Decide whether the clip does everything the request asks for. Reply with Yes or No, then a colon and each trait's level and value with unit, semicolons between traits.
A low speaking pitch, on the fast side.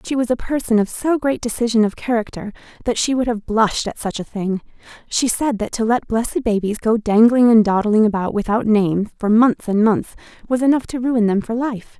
No: high, 225 Hz; fast, 220 wpm